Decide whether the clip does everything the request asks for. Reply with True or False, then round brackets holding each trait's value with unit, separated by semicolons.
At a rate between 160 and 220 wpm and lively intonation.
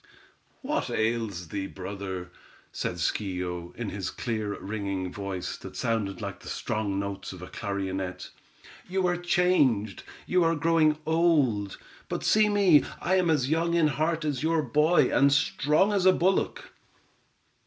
False (150 wpm; 9.0 semitones)